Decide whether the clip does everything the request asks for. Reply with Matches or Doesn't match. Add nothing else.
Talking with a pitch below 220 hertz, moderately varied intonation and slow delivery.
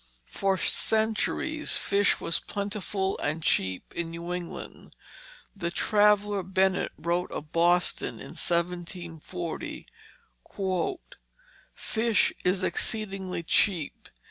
Matches